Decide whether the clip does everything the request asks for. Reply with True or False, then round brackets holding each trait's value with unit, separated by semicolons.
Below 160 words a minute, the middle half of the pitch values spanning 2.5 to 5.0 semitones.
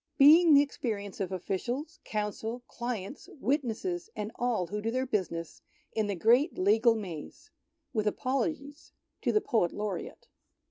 False (145 wpm; 5.4 semitones)